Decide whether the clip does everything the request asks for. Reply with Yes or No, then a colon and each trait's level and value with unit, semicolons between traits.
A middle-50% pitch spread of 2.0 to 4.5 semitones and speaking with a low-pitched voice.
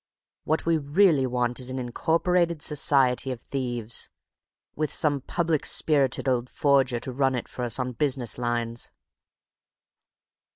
Yes: average, 3.4 semitones; low, 130 Hz